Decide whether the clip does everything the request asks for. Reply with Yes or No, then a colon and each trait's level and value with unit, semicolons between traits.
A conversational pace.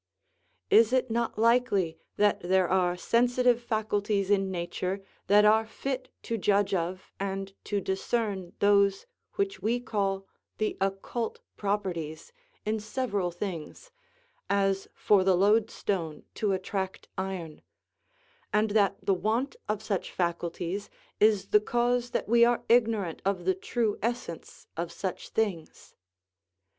No: slow, 130 wpm